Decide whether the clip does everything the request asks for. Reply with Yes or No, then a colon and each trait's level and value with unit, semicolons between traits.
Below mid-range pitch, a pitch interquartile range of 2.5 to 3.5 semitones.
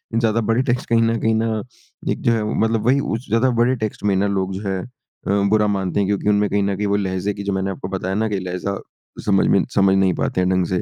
Yes: low, 100 Hz; average, 2.8 semitones